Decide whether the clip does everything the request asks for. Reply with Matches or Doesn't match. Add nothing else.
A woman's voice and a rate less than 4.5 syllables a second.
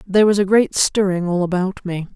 Doesn't match